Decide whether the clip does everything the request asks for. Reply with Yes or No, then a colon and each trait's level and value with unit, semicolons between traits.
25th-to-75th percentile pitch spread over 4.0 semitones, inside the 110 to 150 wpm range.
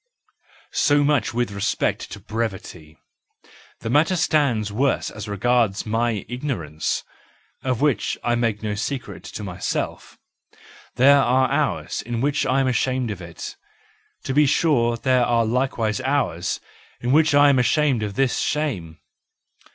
Yes: average, 4.6 semitones; average, 145 wpm